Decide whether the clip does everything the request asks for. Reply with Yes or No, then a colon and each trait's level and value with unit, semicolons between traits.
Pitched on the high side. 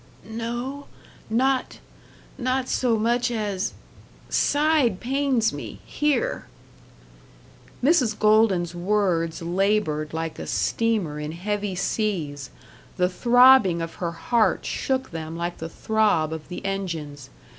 Yes: high, 210 Hz